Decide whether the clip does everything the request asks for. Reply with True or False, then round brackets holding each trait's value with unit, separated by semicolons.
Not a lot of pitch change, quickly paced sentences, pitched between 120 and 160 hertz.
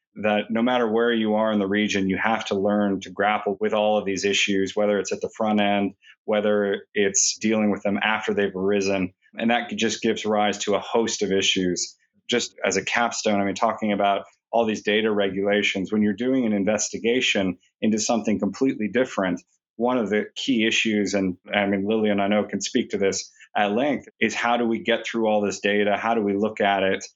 False (1.7 semitones; 215 wpm; 105 Hz)